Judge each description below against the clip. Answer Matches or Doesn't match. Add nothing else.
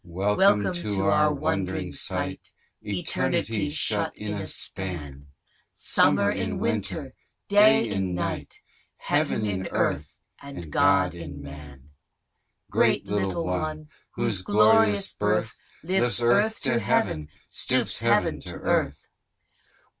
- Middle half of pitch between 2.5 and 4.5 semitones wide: Doesn't match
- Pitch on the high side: Doesn't match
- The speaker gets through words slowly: Matches